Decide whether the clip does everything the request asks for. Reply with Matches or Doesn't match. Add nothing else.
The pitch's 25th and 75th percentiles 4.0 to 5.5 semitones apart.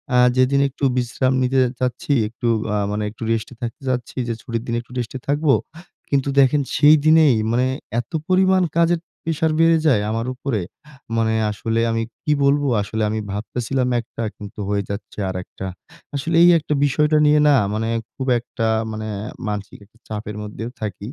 Matches